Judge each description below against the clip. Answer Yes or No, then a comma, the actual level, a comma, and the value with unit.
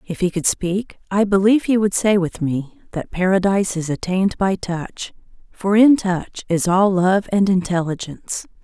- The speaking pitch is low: No, high, 190 Hz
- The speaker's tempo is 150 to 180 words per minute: Yes, average, 175 wpm